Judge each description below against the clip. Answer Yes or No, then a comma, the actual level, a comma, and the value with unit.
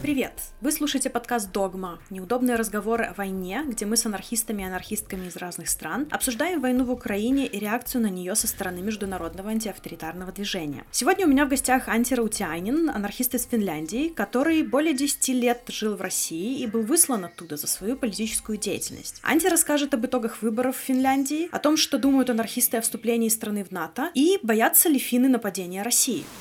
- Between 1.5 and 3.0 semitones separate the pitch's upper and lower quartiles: No, average, 4.7 semitones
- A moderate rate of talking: No, fast, 180 wpm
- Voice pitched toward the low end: No, high, 235 Hz